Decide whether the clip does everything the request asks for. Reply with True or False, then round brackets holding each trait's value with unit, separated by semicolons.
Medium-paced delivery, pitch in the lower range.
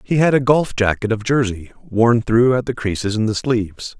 False (225 wpm; 115 Hz)